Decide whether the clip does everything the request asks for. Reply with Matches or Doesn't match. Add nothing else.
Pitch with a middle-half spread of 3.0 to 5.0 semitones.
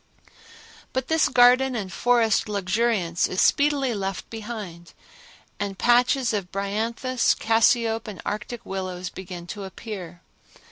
Matches